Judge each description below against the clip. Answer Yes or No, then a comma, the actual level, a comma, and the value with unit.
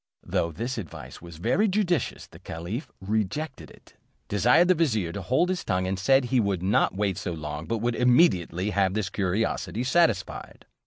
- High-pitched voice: No, low, 105 Hz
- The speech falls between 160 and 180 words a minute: Yes, average, 175 wpm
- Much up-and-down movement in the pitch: Yes, wide, 6.0 semitones